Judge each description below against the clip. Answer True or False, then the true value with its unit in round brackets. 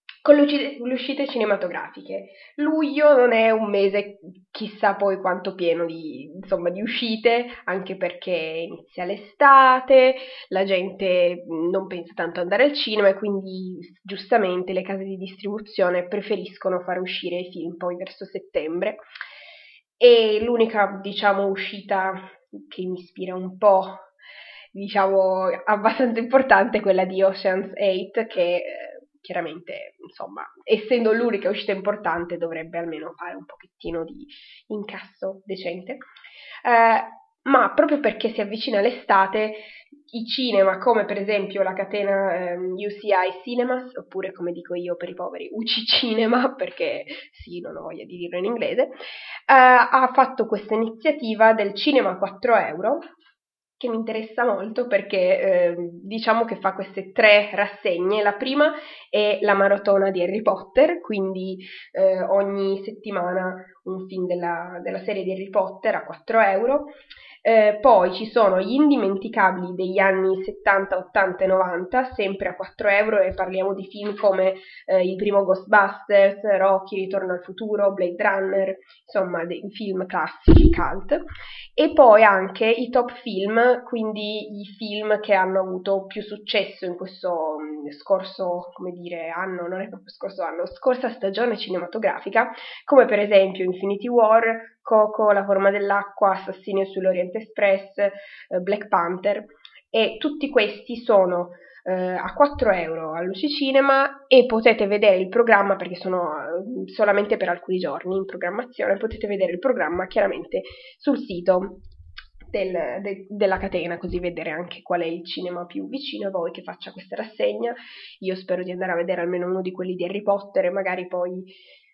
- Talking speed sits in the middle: True (150 wpm)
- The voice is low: False (200 Hz)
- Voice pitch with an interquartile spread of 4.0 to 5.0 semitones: False (3.5 semitones)